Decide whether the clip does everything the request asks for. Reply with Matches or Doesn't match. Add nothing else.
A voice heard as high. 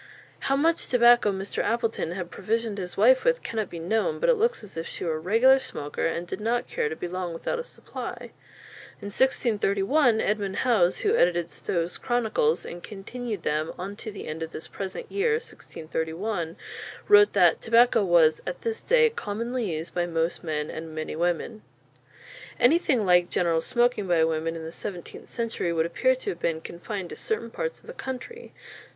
Matches